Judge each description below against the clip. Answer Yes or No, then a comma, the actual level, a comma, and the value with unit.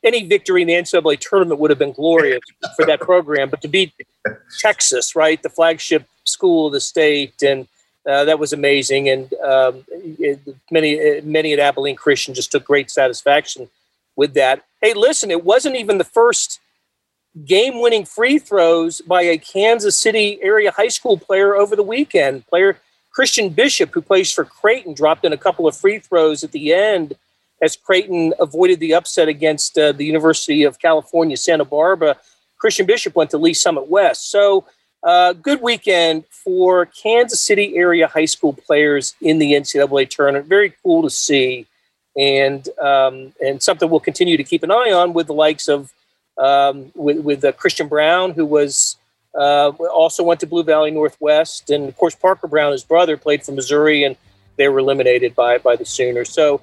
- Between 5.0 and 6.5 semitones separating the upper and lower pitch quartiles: Yes, wide, 5.5 semitones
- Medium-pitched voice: Yes, medium, 160 Hz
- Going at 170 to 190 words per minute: Yes, average, 180 wpm